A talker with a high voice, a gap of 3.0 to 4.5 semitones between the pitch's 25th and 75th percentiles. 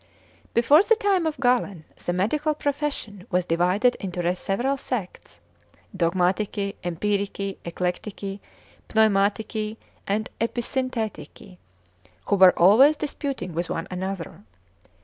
No: high, 205 Hz; wide, 5.5 semitones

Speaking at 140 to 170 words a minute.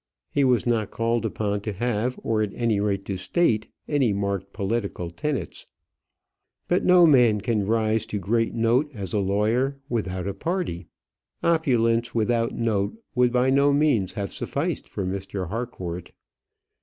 Yes: average, 155 wpm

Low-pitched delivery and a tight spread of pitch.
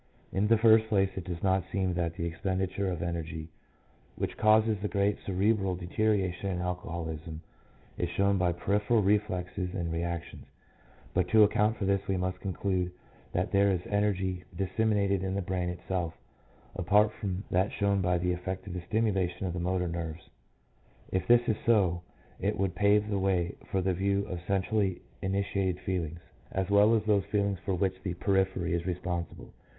Yes: very low, 95 Hz; narrow, 2.2 semitones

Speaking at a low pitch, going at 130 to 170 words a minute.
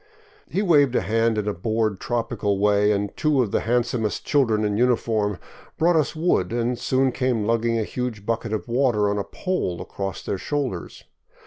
No: low, 115 Hz; average, 185 wpm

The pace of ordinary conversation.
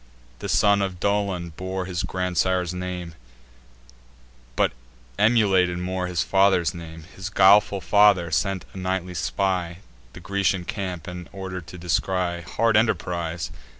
No: slow, 130 wpm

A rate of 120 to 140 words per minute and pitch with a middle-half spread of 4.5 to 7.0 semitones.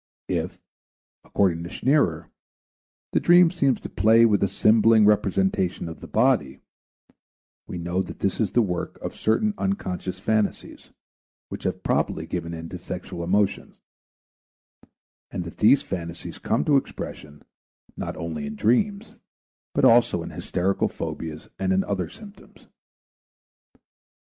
Yes: slow, 135 wpm; average, 4.8 semitones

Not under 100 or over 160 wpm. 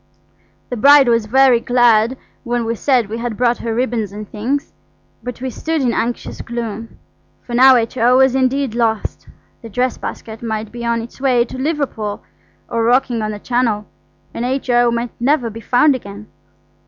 No: average, 175 wpm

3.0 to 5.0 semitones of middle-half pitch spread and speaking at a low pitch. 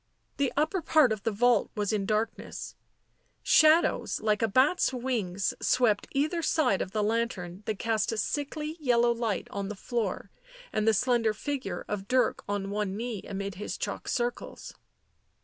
No: average, 4.0 semitones; high, 225 Hz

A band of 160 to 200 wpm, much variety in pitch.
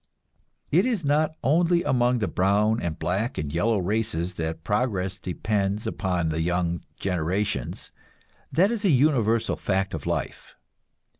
No: average, 140 wpm; wide, 6.1 semitones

